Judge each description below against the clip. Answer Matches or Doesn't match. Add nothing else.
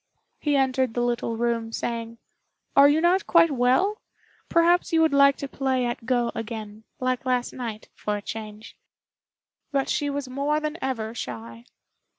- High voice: Matches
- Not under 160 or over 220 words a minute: Matches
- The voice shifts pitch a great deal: Doesn't match